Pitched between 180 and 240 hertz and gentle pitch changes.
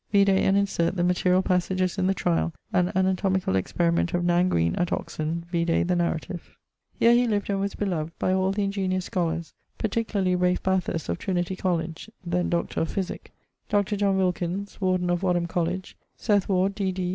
Yes: medium, 185 Hz; narrow, 1.9 semitones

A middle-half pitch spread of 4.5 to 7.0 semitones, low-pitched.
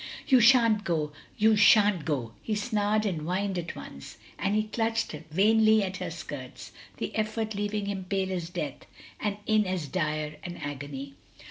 No: average, 5.0 semitones; high, 195 Hz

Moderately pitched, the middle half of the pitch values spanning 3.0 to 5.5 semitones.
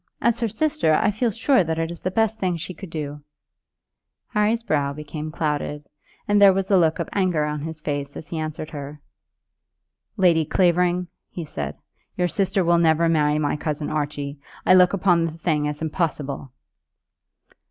Yes: medium, 165 Hz; average, 3.7 semitones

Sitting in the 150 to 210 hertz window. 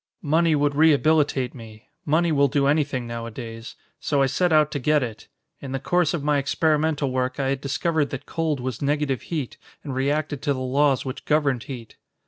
No: medium, 140 Hz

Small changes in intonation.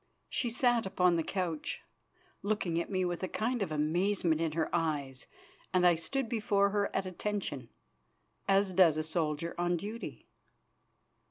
No: average, 3.8 semitones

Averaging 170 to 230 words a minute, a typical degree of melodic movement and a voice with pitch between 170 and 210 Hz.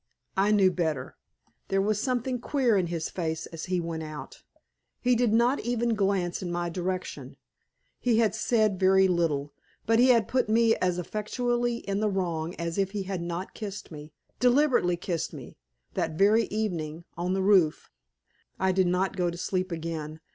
Yes: average, 175 wpm; average, 4.2 semitones; high, 190 Hz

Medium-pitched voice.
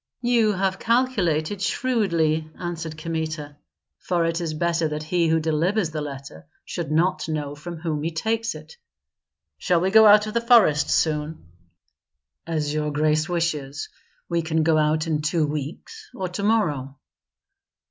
Yes: medium, 165 Hz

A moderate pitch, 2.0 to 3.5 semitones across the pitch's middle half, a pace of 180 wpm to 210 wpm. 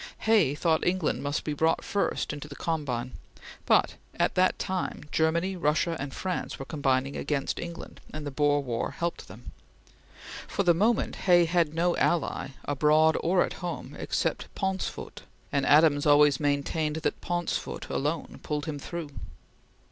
No: medium, 155 Hz; average, 3.1 semitones; average, 155 wpm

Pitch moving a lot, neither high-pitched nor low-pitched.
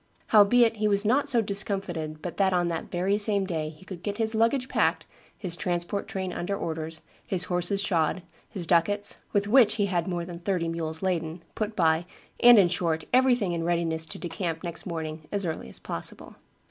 No: average, 3.5 semitones; medium, 180 Hz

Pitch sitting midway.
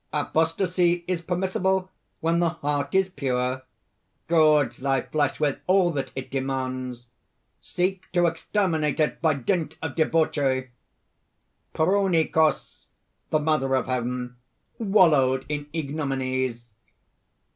Yes: medium, 155 Hz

